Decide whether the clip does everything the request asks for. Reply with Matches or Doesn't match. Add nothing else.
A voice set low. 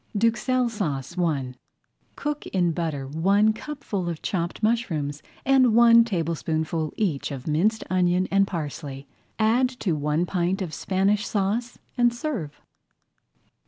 Doesn't match